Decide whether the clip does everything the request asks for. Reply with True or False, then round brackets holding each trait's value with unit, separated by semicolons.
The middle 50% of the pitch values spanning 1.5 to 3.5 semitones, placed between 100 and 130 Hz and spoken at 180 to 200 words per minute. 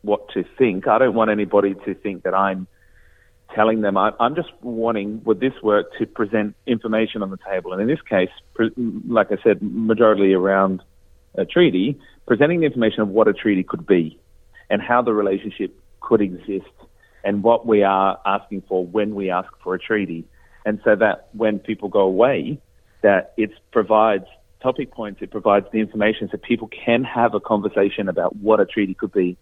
True (2.6 semitones; 105 Hz; 190 wpm)